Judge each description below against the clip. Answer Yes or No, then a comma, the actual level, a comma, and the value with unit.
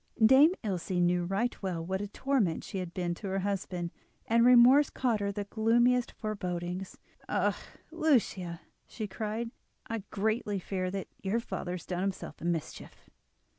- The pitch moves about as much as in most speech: Yes, average, 4.2 semitones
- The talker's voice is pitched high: Yes, high, 200 Hz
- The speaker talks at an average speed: Yes, average, 160 wpm